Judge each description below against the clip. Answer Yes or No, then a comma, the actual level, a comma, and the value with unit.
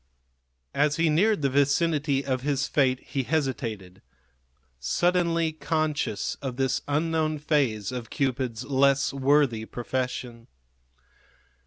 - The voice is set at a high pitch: No, medium, 140 Hz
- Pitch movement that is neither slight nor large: Yes, average, 3.2 semitones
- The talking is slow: Yes, slow, 110 wpm